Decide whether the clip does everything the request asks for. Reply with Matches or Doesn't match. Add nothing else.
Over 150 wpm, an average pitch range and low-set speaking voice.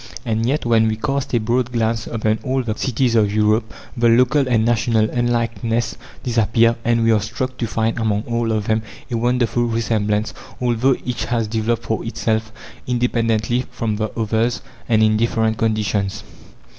Doesn't match